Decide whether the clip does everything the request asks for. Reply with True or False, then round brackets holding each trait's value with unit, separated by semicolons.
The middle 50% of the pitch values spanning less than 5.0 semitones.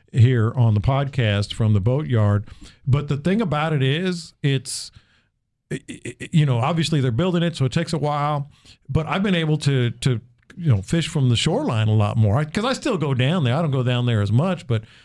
False (5.3 semitones)